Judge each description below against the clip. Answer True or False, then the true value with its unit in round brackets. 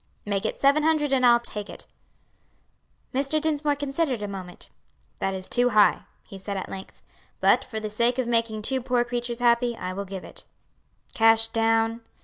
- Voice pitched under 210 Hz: False (235 Hz)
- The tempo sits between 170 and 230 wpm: True (180 wpm)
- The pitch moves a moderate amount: True (3.6 semitones)